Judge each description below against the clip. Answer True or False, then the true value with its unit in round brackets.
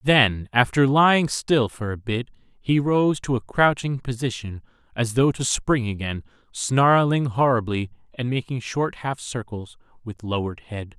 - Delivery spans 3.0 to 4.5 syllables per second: True (4.3 syllables/s)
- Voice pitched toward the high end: False (125 Hz)